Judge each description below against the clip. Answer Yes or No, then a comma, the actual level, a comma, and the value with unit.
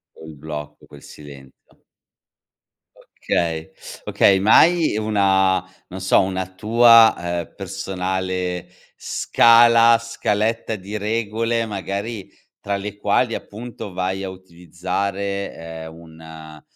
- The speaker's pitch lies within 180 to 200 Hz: No, very low, 95 Hz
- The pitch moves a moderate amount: Yes, average, 3.9 semitones